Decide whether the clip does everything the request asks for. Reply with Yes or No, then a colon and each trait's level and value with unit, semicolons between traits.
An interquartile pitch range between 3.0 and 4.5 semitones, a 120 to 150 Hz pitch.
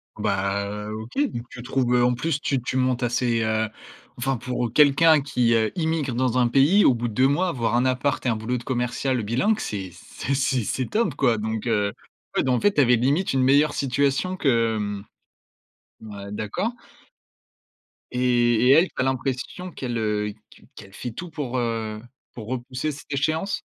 Yes: average, 3.5 semitones; low, 125 Hz